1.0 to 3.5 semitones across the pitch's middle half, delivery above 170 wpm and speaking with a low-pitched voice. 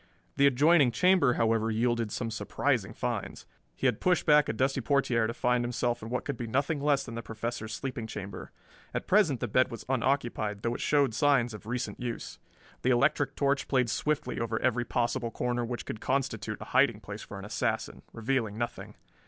Yes: average, 3.2 semitones; average, 195 wpm; low, 120 Hz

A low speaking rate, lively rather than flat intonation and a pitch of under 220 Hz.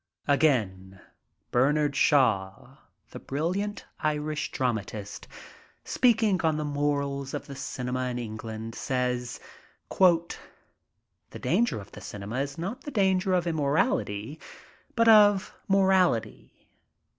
Yes: slow, 110 wpm; wide, 7.1 semitones; medium, 140 Hz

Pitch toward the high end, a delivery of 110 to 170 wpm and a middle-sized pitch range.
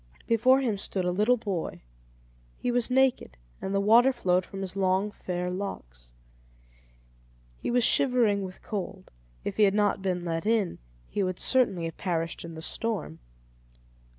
Yes: high, 195 Hz; average, 160 wpm; average, 4.2 semitones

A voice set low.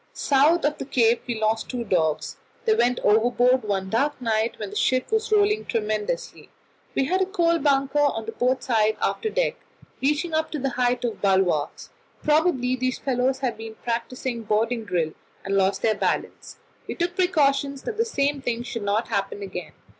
No: very high, 250 Hz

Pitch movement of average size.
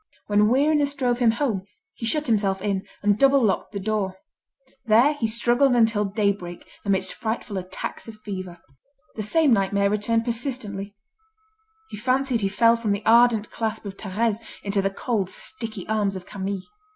Yes: average, 3.0 semitones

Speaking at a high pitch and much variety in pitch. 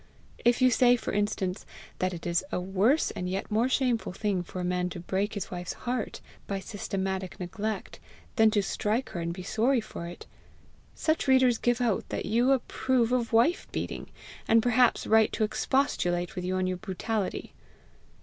No: high, 210 Hz; average, 4.8 semitones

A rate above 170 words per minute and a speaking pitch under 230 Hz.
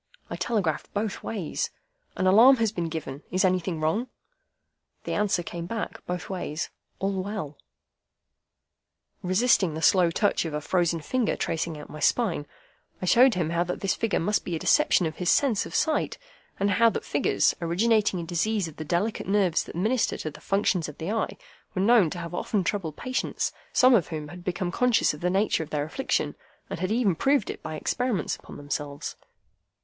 Yes: average, 190 wpm; medium, 185 Hz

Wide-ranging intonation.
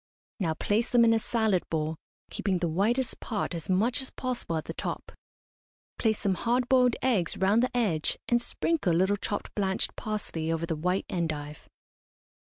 Yes: wide, 5.9 semitones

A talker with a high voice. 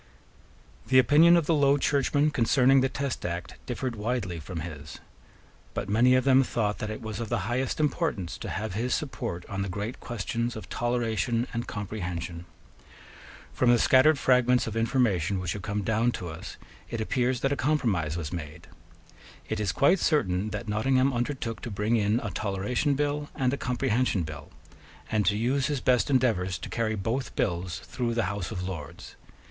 No: low, 115 Hz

